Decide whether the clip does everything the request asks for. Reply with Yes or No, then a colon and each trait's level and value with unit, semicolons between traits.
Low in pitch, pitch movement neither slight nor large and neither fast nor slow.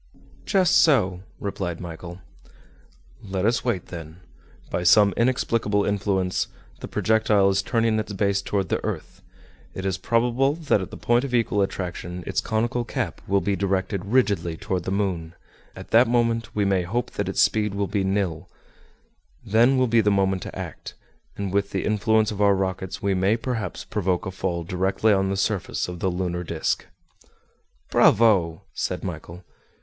Yes: low, 100 Hz; average, 3.1 semitones; average, 170 wpm